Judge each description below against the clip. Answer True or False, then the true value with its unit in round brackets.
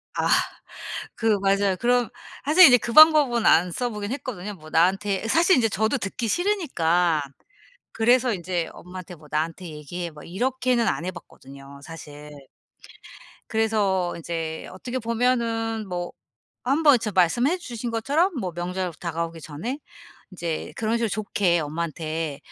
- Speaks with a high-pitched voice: True (195 Hz)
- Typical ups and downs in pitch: False (6.2 semitones)